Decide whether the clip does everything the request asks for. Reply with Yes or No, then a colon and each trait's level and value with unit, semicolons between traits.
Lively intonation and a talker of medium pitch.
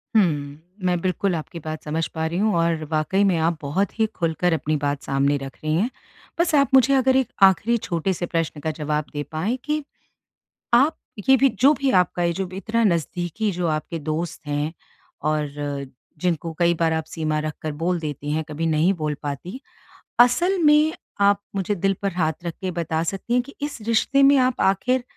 Yes: wide, 5.8 semitones; medium, 175 Hz